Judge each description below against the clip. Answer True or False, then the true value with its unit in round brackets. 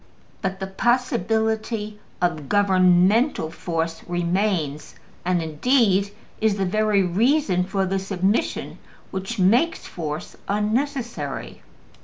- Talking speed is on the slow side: True (100 wpm)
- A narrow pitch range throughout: False (3.8 semitones)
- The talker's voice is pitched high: True (195 Hz)